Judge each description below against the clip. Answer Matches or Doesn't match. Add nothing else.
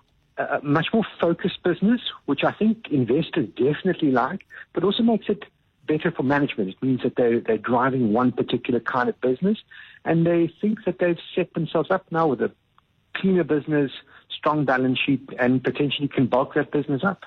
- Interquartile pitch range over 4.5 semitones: Matches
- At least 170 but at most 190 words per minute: Matches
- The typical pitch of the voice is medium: Matches